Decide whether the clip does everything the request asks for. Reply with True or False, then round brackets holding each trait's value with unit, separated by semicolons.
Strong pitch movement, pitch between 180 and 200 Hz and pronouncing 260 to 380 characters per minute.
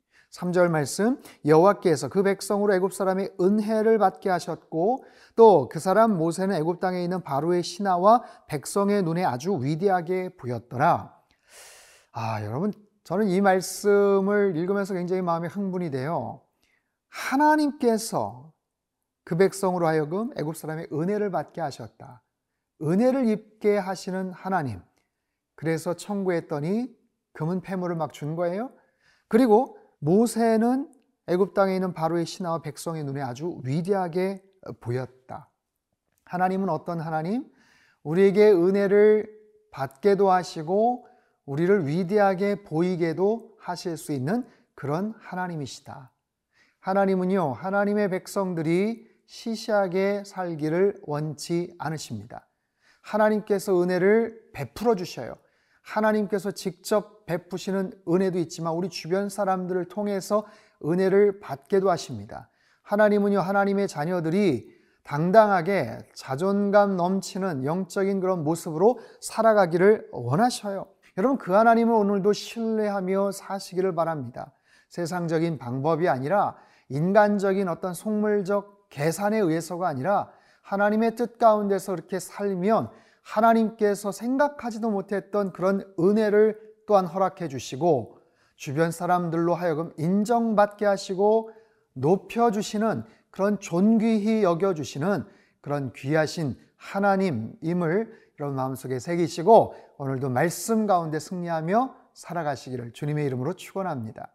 False (3.8 semitones; 190 Hz; 295 characters per minute)